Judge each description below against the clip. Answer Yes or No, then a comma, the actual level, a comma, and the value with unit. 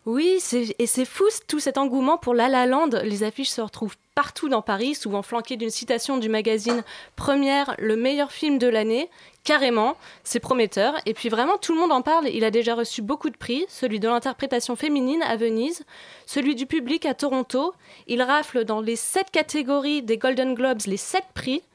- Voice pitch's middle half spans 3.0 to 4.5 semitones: Yes, average, 3.9 semitones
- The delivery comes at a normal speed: Yes, average, 200 wpm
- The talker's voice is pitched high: Yes, very high, 260 Hz